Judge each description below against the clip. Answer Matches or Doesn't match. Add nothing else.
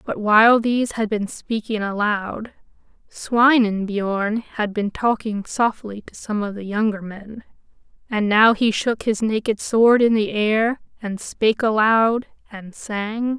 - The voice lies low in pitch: Doesn't match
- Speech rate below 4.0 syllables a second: Matches